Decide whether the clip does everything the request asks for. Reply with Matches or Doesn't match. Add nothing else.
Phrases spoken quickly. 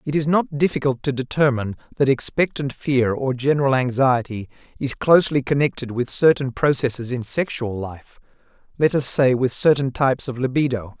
Doesn't match